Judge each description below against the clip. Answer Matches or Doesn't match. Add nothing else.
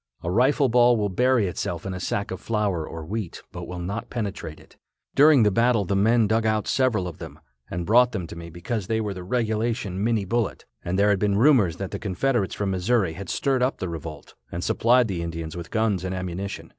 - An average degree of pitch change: Matches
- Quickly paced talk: Matches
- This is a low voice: Matches